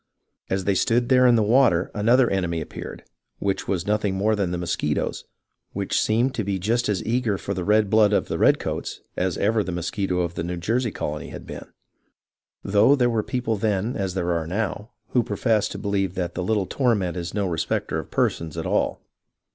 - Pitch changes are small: No, average, 3.8 semitones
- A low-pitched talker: Yes, low, 100 Hz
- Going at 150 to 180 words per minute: No, fast, 205 wpm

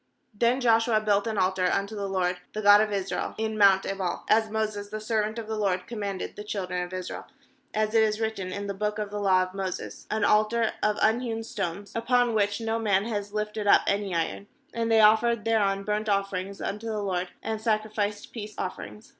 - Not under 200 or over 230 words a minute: Yes, fast, 205 wpm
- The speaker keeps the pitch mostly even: Yes, narrow, 1.9 semitones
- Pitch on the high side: Yes, high, 210 Hz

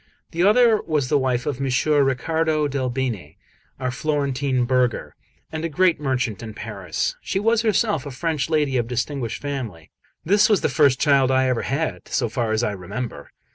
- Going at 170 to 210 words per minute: Yes, average, 180 wpm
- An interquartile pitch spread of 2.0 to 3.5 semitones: No, average, 4.2 semitones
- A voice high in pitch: No, low, 135 Hz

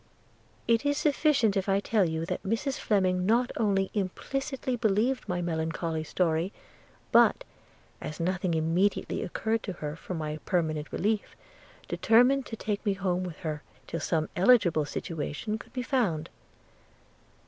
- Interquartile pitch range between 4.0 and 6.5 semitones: Yes, wide, 5.5 semitones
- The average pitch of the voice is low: No, high, 190 Hz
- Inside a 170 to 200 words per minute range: No, average, 145 wpm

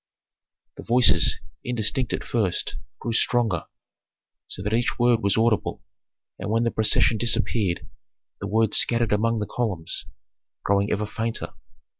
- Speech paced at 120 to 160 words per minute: Yes, average, 145 wpm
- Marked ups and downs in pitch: No, narrow, 2.6 semitones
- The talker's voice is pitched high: No, low, 110 Hz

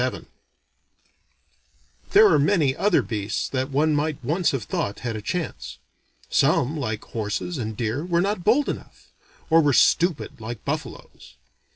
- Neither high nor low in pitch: Yes, medium, 145 Hz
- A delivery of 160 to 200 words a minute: No, average, 150 wpm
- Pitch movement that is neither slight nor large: No, wide, 7.3 semitones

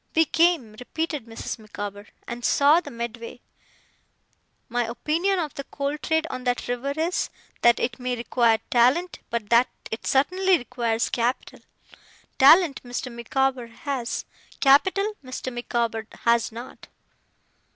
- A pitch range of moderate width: Yes, average, 4.2 semitones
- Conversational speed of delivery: No, slow, 130 wpm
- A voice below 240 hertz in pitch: No, very high, 250 Hz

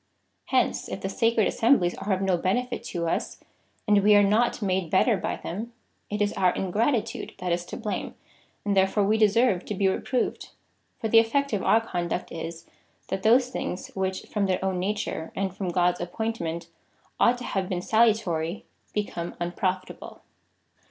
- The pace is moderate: Yes, average, 180 wpm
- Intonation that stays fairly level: No, average, 3.6 semitones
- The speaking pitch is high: Yes, high, 195 Hz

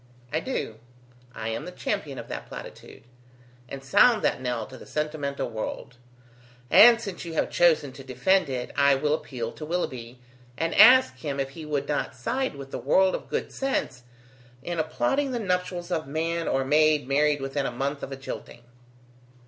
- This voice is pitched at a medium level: Yes, medium, 145 Hz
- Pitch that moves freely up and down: No, average, 4.6 semitones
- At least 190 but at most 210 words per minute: No, average, 180 wpm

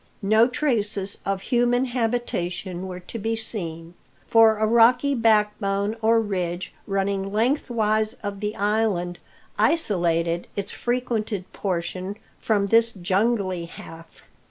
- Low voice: No, high, 210 Hz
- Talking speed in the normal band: No, slow, 115 wpm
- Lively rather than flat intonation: No, average, 3.3 semitones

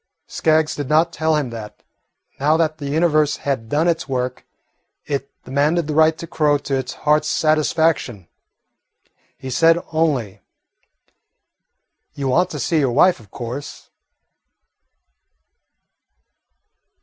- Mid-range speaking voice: Yes, medium, 150 Hz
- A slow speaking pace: Yes, slow, 125 wpm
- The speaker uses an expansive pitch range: No, average, 3.1 semitones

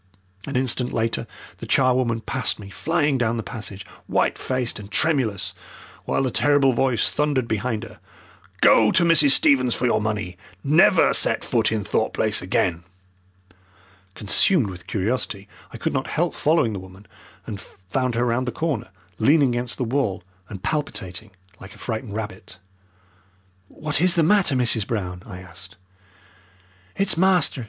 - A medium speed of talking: Yes, average, 155 wpm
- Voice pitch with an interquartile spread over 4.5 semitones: Yes, average, 5.1 semitones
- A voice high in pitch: No, low, 120 Hz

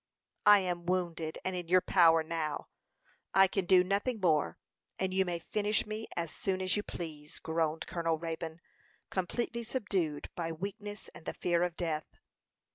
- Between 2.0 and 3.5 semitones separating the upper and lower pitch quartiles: Yes, average, 2.9 semitones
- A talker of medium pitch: Yes, medium, 175 Hz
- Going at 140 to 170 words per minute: Yes, average, 165 wpm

